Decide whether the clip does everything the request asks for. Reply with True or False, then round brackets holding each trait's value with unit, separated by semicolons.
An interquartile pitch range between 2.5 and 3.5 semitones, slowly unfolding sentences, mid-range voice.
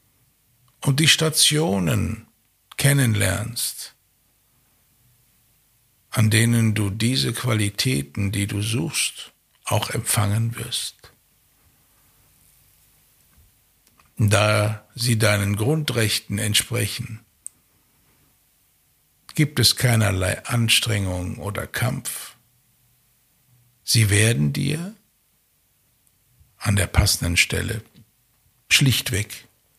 False (3.0 semitones; 70 wpm; 115 Hz)